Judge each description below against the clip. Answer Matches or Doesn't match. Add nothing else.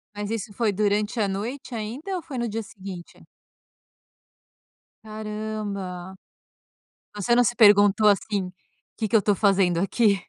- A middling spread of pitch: Doesn't match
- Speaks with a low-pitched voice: Doesn't match